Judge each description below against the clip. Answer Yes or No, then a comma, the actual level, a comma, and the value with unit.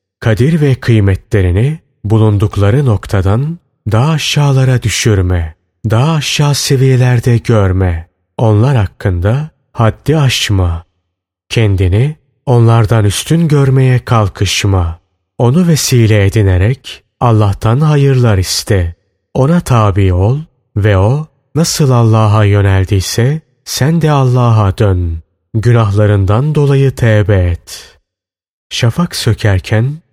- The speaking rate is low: Yes, slow, 90 wpm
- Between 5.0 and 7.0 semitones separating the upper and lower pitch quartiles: Yes, average, 5.3 semitones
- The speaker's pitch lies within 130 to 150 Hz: No, low, 110 Hz